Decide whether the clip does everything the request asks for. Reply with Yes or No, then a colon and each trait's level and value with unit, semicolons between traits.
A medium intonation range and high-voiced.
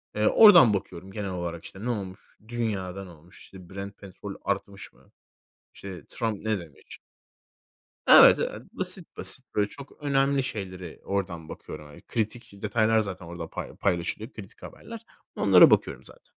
No: average, 3.5 semitones; low, 100 Hz